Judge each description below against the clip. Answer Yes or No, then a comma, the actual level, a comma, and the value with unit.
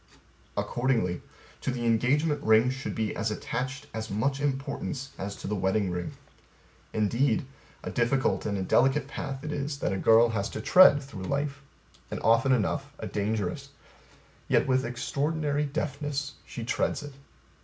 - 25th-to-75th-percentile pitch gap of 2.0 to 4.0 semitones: No, average, 4.4 semitones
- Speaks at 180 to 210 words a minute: No, average, 155 wpm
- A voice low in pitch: Yes, low, 130 Hz